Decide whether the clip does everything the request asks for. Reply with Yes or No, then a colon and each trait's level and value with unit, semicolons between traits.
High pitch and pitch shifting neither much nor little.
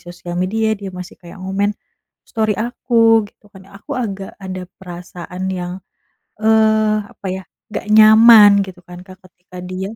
Yes: high, 195 Hz; average, 3.1 semitones